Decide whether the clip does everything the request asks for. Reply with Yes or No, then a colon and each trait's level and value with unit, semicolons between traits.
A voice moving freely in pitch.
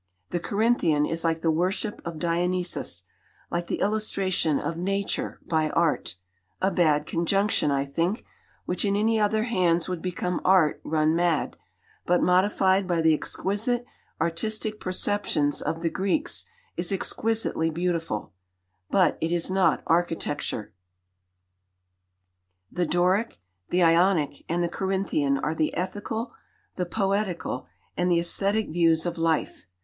No: average, 3.2 semitones